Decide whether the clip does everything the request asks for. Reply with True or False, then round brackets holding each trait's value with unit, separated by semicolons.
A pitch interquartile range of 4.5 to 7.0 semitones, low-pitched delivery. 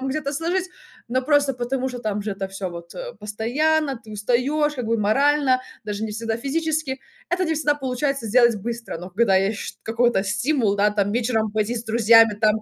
False (4.8 semitones; 235 Hz)